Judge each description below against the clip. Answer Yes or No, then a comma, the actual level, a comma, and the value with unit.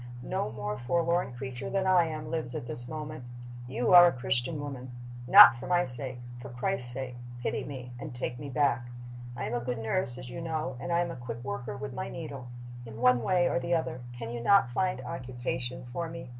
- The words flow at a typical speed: No, fast, 215 wpm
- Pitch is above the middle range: No, low, 130 Hz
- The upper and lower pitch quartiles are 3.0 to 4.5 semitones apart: No, average, 5.1 semitones